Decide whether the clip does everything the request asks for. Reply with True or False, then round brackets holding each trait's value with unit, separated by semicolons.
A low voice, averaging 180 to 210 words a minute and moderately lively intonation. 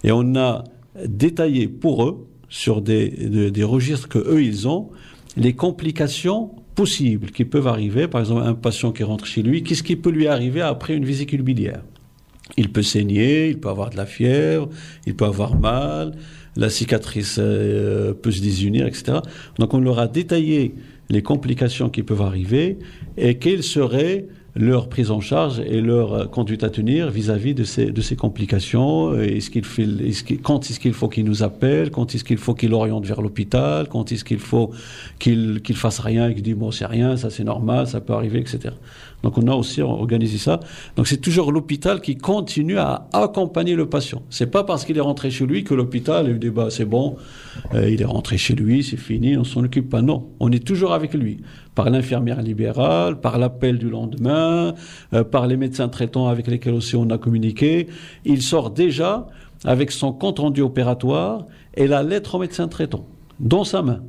True (125 Hz; 195 wpm; 4.4 semitones)